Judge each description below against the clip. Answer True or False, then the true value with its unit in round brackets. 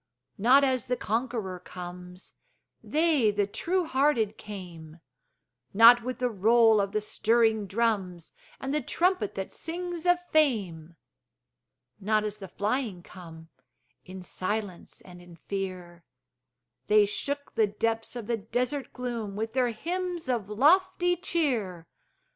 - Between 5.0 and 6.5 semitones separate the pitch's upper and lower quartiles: True (5.4 semitones)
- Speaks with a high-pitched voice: True (220 Hz)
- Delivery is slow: True (130 wpm)